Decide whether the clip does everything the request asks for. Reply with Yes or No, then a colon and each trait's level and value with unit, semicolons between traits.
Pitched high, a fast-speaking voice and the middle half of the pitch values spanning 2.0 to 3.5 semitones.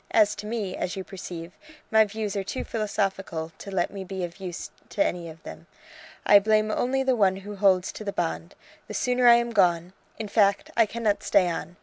Yes: high, 200 Hz; fast, 215 wpm; average, 3.2 semitones